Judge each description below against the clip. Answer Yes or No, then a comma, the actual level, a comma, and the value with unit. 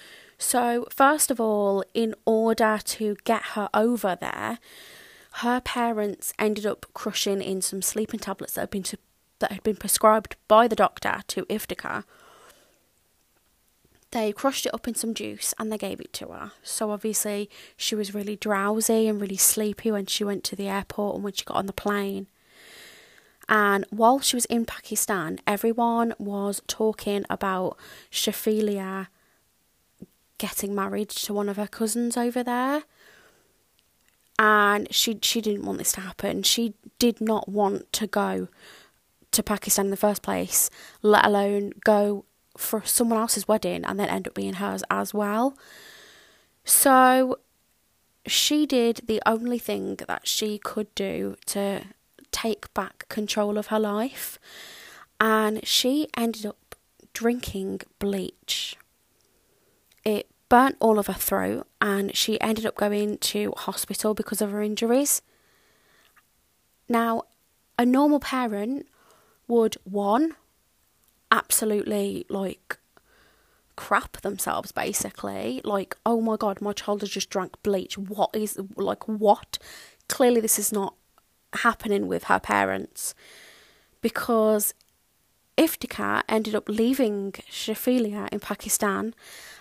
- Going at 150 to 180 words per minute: No, slow, 135 wpm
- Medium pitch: No, high, 215 Hz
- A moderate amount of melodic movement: No, narrow, 2.1 semitones